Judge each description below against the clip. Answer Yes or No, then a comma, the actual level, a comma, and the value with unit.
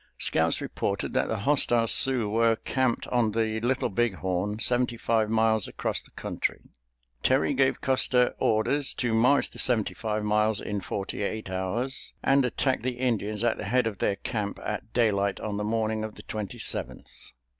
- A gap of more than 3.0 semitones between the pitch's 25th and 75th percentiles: No, average, 2.7 semitones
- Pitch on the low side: Yes, low, 110 Hz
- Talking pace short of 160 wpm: No, average, 175 wpm